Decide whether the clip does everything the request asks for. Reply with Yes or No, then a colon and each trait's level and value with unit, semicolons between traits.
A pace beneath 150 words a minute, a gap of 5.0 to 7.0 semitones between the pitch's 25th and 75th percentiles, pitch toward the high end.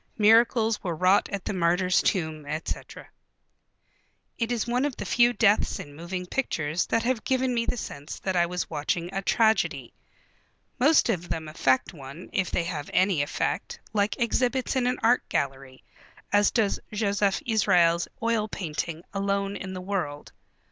No: average, 160 wpm; average, 5.3 semitones; high, 195 Hz